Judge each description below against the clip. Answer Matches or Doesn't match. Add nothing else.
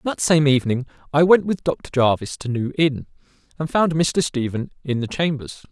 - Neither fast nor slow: Matches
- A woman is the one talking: Doesn't match